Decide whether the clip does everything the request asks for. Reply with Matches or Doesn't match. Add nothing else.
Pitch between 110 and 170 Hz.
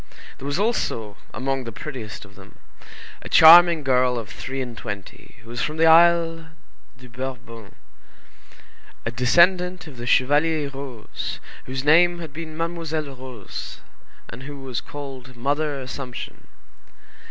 Matches